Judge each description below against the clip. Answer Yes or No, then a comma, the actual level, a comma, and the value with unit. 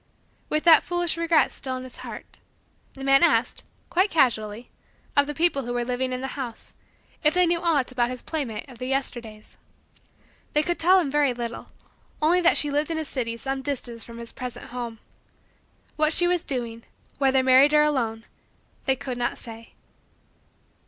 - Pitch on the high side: Yes, very high, 270 Hz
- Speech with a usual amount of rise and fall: Yes, average, 4.2 semitones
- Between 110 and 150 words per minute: No, average, 180 wpm